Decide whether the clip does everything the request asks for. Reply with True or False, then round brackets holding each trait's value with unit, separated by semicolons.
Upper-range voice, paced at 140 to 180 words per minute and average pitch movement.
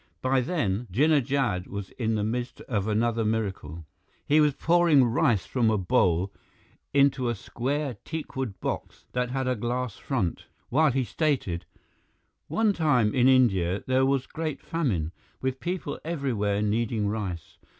False (125 Hz; 150 wpm; 4.9 semitones)